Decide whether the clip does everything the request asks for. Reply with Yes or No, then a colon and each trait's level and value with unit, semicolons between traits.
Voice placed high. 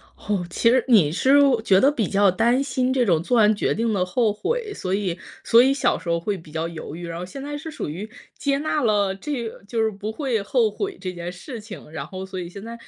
Yes: high, 210 Hz